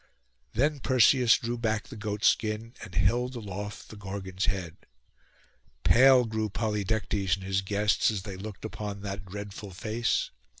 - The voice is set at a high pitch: No, low, 105 Hz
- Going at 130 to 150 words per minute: Yes, average, 145 wpm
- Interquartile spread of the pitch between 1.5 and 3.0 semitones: Yes, average, 2.7 semitones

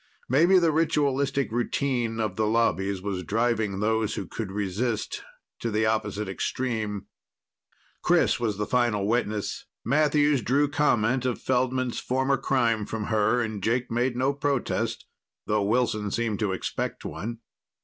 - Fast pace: No, average, 140 wpm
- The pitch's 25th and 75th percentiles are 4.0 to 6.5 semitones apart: No, average, 3.5 semitones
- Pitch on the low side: Yes, low, 115 Hz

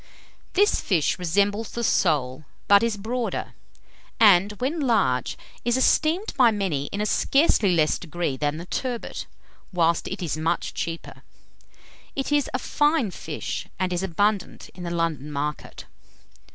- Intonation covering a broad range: Yes, wide, 6.1 semitones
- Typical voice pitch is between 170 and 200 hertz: Yes, high, 190 Hz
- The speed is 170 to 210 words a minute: No, average, 145 wpm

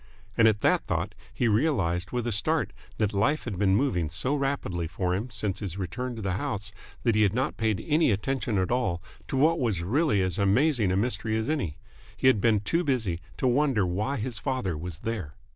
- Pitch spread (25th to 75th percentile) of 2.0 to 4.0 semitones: No, average, 5.3 semitones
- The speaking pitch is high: No, low, 110 Hz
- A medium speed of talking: No, fast, 210 wpm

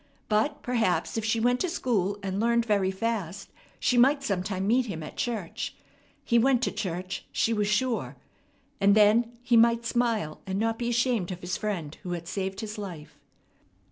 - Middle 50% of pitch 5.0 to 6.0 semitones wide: No, average, 3.7 semitones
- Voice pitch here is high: Yes, high, 215 Hz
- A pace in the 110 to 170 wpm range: No, average, 180 wpm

